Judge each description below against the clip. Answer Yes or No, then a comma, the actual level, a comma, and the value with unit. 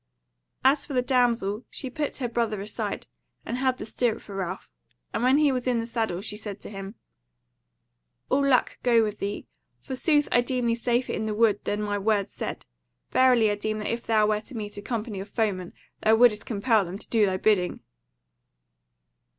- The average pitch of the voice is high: Yes, high, 220 Hz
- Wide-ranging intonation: No, average, 3.2 semitones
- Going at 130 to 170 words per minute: No, average, 200 wpm